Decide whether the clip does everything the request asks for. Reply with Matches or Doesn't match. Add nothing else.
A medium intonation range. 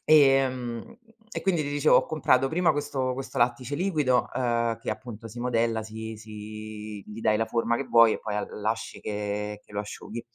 Matches